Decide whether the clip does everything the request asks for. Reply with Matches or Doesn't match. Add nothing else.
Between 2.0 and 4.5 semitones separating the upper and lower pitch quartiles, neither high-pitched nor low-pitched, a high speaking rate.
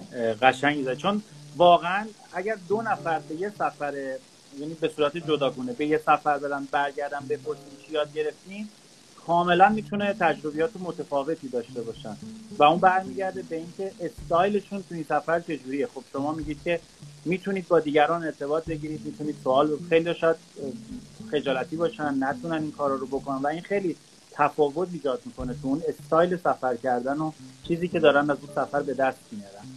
Matches